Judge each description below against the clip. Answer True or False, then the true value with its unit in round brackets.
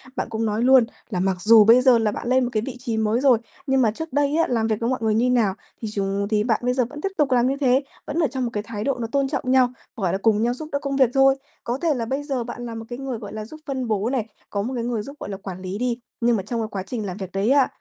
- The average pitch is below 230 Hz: False (235 Hz)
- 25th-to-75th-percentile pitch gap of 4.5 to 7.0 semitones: False (3.5 semitones)